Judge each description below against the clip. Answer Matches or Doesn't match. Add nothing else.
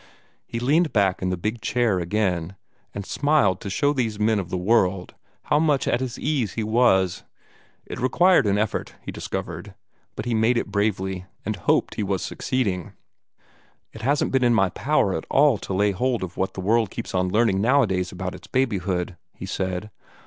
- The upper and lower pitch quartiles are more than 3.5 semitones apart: Matches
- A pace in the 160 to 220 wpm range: Matches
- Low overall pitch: Matches